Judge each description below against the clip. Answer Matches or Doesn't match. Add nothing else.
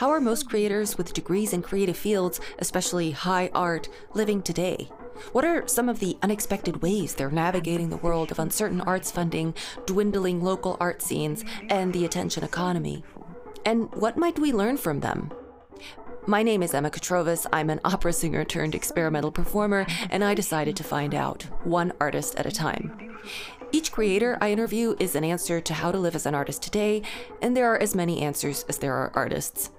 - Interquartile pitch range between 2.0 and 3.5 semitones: Doesn't match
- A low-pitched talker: Doesn't match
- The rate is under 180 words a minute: Doesn't match